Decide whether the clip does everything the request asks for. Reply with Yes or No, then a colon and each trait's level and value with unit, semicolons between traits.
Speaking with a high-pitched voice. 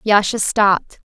Yes: high, 205 Hz